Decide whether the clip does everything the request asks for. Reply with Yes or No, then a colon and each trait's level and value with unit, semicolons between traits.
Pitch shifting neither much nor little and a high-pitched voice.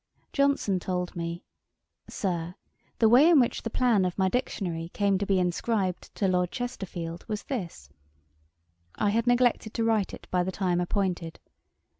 Yes: average, 4.3 semitones; high, 195 Hz